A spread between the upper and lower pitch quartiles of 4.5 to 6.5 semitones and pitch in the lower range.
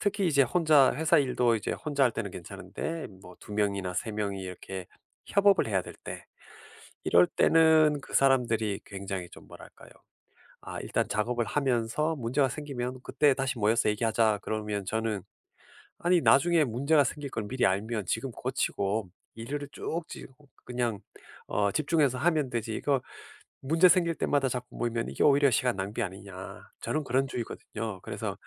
Yes: wide, 5.5 semitones; low, 125 Hz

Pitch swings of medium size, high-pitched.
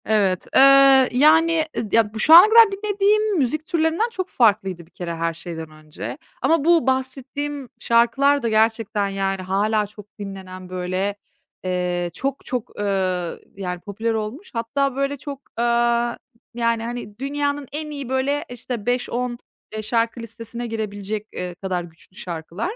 No: wide, 6.0 semitones; high, 230 Hz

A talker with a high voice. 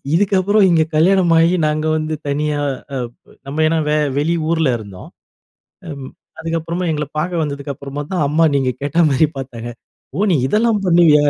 No: medium, 155 Hz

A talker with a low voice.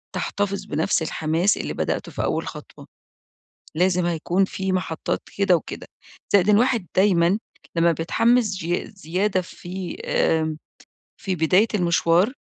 No: medium, 185 Hz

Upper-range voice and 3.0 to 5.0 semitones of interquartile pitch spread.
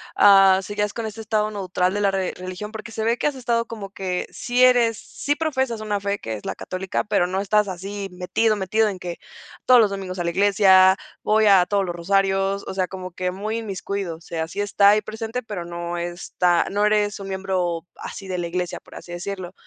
No: high, 195 Hz; narrow, 2.6 semitones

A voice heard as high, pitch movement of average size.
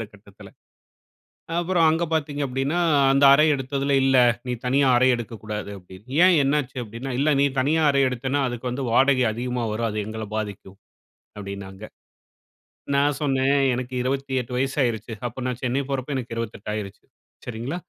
No: low, 130 Hz; average, 3.6 semitones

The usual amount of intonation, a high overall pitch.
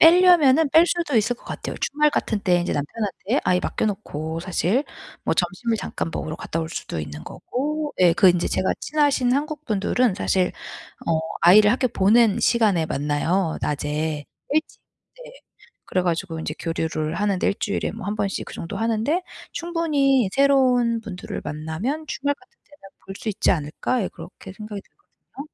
No: wide, 8.0 semitones; high, 210 Hz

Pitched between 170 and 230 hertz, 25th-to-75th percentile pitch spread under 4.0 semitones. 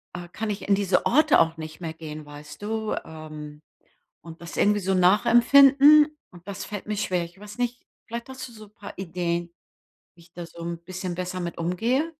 No: medium, 185 Hz; average, 4.7 semitones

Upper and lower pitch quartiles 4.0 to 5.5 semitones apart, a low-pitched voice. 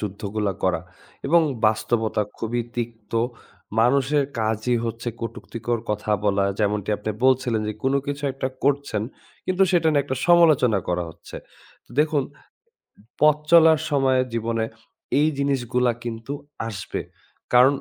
Yes: average, 4.5 semitones; low, 120 Hz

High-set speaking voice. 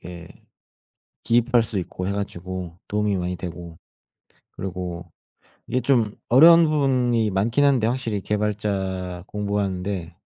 No: low, 100 Hz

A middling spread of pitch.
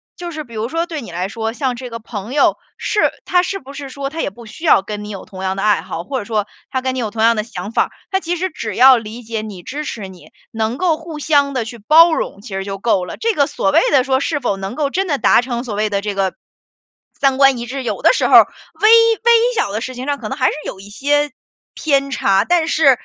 No: wide, 5.7 semitones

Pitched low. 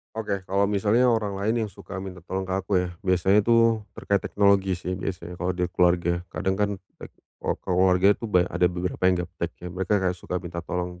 Yes: very low, 95 Hz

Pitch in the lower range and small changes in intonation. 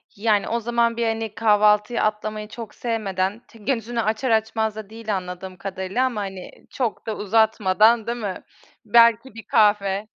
No: high, 215 Hz; narrow, 2.0 semitones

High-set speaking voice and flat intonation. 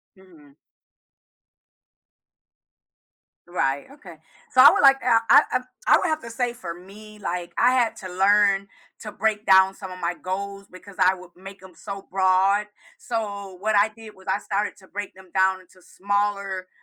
Yes: high, 195 Hz; narrow, 2.1 semitones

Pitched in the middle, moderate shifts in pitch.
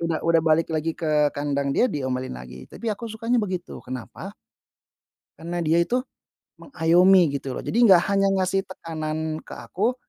Yes: medium, 165 Hz; average, 4.2 semitones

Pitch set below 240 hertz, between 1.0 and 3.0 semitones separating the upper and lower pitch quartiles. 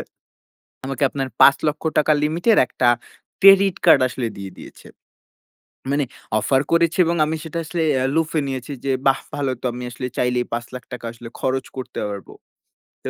No: low, 135 Hz; average, 4.3 semitones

